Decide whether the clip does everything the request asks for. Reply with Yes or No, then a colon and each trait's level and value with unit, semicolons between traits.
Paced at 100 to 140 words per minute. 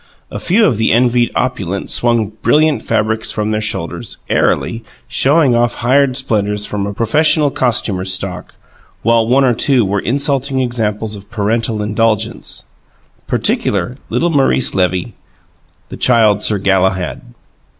Yes: slow, 135 wpm